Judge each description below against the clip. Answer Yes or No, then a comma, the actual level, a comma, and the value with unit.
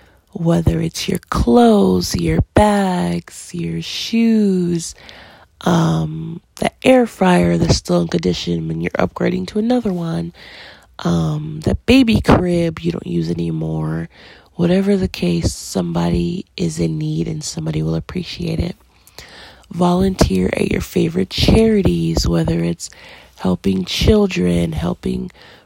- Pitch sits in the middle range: Yes, medium, 155 Hz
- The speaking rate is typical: No, slow, 120 wpm